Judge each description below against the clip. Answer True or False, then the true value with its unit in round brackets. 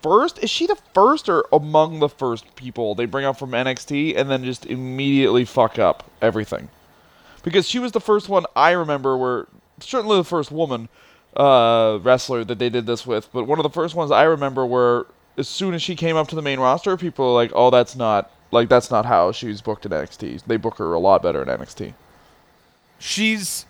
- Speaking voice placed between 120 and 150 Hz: True (135 Hz)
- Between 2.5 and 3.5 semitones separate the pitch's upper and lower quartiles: False (5.4 semitones)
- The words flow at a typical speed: False (215 wpm)